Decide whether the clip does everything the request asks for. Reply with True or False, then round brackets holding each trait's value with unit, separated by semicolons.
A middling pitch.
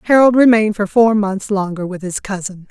False (205 Hz)